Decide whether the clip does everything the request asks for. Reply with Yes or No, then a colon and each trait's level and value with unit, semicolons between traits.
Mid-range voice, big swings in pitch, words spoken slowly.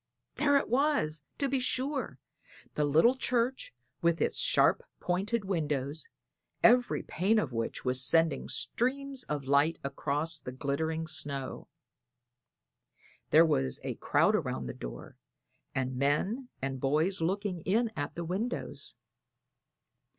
Yes: medium, 165 Hz; wide, 8.8 semitones; slow, 130 wpm